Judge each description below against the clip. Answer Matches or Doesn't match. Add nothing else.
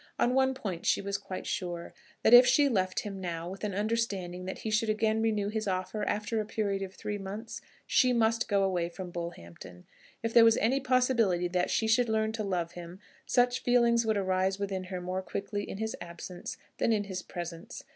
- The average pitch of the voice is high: Matches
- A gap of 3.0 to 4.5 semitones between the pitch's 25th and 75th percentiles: Matches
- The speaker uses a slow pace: Doesn't match